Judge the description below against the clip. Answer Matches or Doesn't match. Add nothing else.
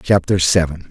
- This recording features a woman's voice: Doesn't match